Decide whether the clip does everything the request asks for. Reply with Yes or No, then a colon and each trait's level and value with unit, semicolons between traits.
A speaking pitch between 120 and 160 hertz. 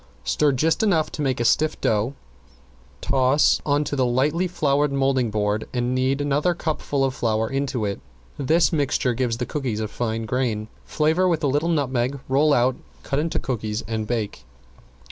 Yes: low, 135 Hz